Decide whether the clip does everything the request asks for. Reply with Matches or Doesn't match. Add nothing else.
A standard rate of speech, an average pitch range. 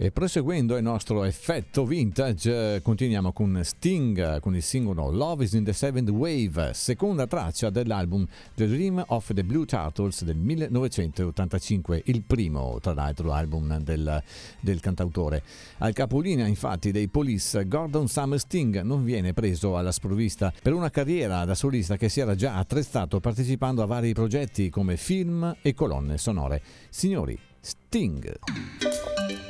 Doesn't match